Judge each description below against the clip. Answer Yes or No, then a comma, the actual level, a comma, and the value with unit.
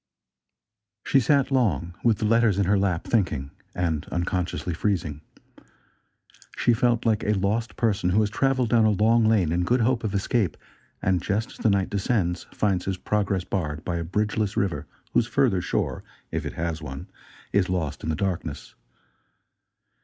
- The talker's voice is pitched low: Yes, low, 100 Hz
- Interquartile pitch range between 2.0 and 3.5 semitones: No, average, 4.2 semitones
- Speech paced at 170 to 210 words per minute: Yes, average, 175 wpm